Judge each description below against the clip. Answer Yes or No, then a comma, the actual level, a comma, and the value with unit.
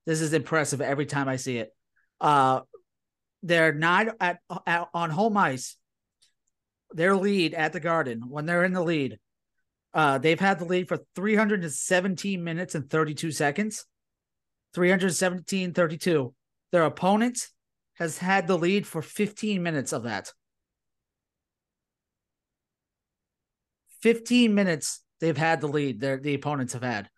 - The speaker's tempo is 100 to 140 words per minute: Yes, slow, 135 wpm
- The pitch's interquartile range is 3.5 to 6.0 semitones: Yes, average, 4.2 semitones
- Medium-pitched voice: Yes, medium, 170 Hz